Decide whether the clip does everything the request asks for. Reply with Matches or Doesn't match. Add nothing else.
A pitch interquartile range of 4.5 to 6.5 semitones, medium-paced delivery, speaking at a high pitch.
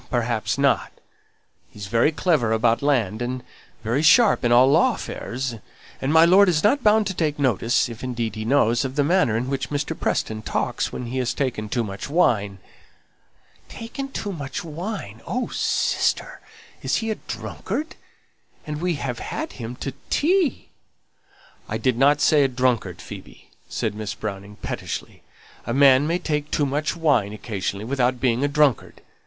Doesn't match